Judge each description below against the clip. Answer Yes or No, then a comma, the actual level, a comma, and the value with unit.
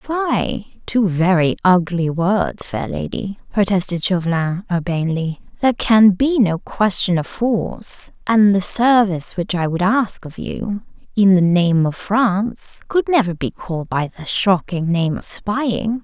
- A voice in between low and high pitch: No, high, 195 Hz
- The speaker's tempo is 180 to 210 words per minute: No, average, 155 wpm